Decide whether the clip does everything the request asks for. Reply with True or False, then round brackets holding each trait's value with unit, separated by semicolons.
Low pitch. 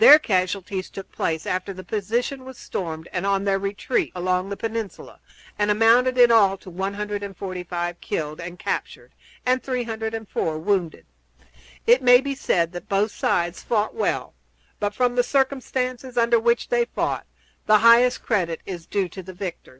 False (205 Hz)